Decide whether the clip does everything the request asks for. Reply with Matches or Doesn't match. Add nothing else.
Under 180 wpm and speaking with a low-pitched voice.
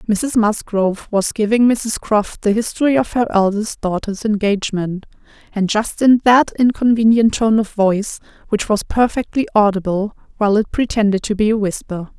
Doesn't match